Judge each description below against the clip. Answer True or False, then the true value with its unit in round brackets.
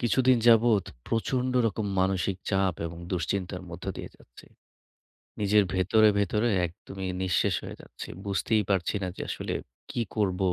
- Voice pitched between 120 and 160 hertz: False (100 Hz)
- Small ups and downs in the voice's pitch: False (3.1 semitones)